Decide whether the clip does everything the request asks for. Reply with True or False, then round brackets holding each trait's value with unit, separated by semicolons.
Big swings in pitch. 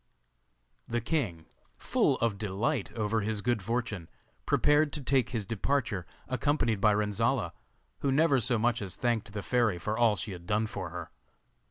False (3.2 semitones)